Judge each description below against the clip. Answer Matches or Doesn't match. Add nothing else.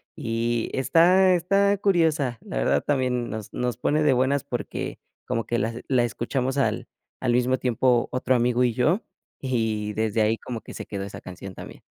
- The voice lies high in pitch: Doesn't match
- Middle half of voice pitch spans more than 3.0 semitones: Matches